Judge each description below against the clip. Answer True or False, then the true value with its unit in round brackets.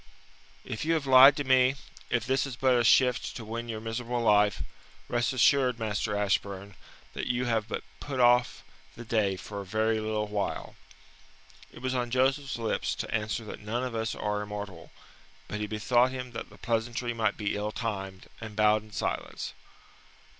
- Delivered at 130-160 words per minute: False (180 wpm)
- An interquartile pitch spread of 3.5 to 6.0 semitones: False (3.0 semitones)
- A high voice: False (115 Hz)